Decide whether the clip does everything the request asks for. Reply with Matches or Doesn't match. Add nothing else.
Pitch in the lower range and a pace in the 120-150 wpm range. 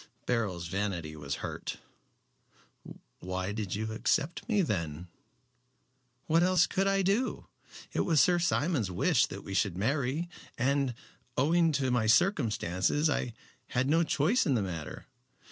Matches